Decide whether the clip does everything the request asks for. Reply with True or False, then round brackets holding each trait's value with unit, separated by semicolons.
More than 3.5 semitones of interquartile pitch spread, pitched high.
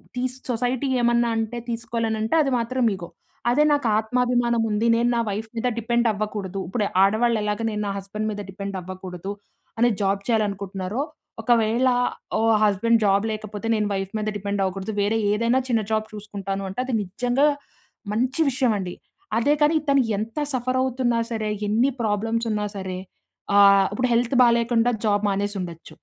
False (3.1 semitones; 220 Hz)